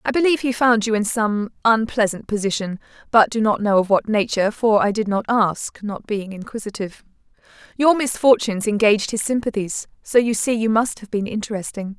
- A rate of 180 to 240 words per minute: Yes, average, 185 wpm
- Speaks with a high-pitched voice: Yes, high, 215 Hz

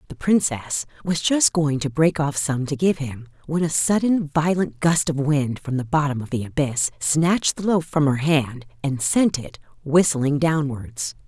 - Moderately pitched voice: Yes, medium, 150 Hz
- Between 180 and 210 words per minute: Yes, average, 190 wpm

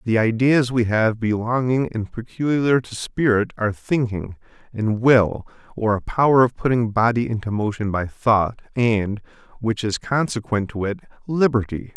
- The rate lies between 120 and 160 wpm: Yes, average, 150 wpm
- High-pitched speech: No, low, 115 Hz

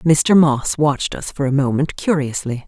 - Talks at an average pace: Yes, average, 180 wpm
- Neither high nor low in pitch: Yes, medium, 145 Hz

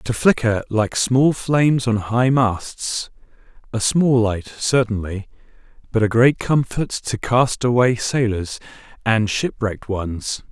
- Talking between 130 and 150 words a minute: Yes, slow, 135 wpm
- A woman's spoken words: No, male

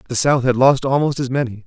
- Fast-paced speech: Yes, fast, 255 wpm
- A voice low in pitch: Yes, low, 130 Hz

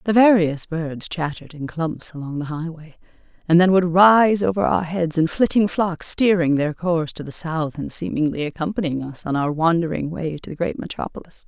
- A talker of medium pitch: Yes, medium, 165 Hz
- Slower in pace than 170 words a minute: No, average, 195 wpm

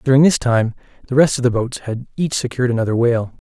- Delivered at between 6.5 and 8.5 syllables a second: Yes, 6.6 syllables/s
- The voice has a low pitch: Yes, low, 125 Hz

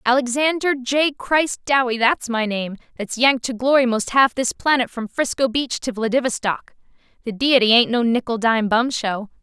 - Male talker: No, female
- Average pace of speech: Yes, average, 170 wpm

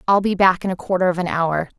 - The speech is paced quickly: Yes, fast, 305 wpm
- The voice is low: No, medium, 180 Hz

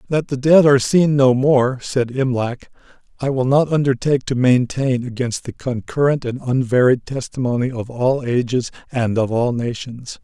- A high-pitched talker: No, low, 130 Hz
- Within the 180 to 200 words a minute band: No, average, 165 wpm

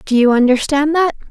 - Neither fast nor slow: Yes, average, 185 wpm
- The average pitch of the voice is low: No, very high, 280 Hz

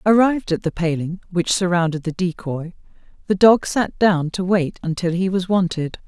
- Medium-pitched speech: Yes, medium, 180 Hz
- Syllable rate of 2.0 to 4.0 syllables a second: No, 4.9 syllables/s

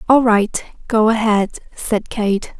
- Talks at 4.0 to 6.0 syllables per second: No, 3.5 syllables/s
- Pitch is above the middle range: Yes, high, 220 Hz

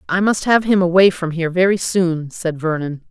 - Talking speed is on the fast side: Yes, fast, 215 wpm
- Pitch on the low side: No, medium, 175 Hz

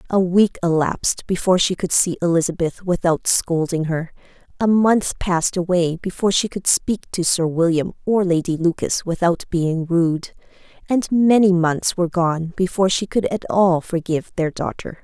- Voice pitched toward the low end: No, medium, 175 Hz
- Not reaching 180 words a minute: Yes, average, 165 wpm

